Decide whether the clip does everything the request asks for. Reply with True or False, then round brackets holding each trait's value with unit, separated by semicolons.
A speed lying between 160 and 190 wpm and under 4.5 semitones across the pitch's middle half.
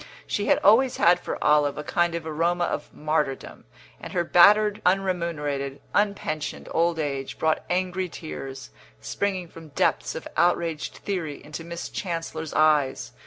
False (150 wpm; 3.1 semitones)